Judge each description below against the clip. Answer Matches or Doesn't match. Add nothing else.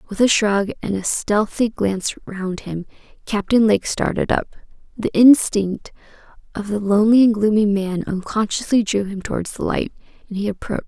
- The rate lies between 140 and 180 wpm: Matches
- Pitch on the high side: Matches